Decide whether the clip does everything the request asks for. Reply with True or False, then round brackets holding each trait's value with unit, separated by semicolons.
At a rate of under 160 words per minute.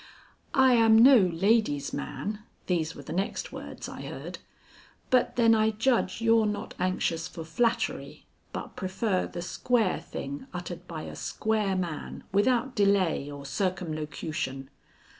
True (140 wpm)